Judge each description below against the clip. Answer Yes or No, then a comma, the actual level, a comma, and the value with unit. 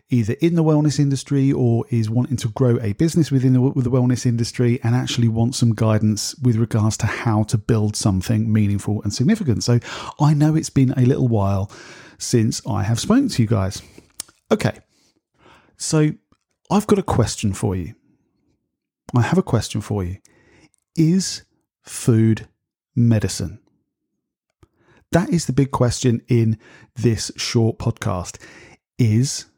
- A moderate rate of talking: Yes, average, 150 wpm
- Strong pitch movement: No, average, 3.6 semitones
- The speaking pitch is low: Yes, low, 120 Hz